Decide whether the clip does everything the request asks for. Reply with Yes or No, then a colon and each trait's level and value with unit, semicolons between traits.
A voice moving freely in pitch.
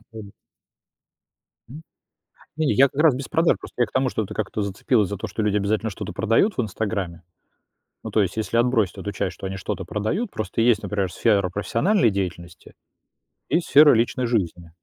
No: average, 4.2 semitones